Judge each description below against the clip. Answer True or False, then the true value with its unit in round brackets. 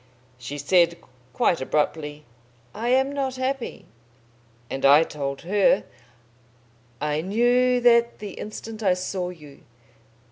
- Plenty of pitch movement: True (8.2 semitones)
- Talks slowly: True (115 wpm)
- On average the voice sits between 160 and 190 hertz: True (185 Hz)